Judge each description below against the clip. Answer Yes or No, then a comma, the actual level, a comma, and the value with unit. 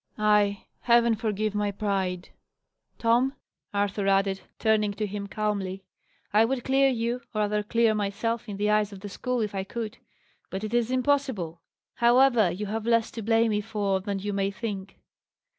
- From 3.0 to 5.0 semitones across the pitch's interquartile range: No, narrow, 2.5 semitones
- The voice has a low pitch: No, high, 210 Hz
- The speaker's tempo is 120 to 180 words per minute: Yes, average, 175 wpm